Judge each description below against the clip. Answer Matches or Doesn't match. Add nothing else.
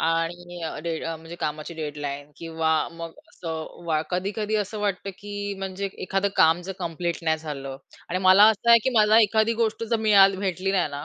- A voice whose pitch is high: Doesn't match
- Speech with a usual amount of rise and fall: Matches